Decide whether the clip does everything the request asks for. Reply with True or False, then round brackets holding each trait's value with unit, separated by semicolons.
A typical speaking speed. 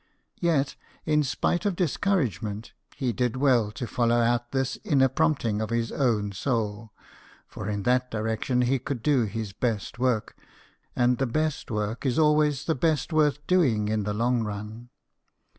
True (160 wpm)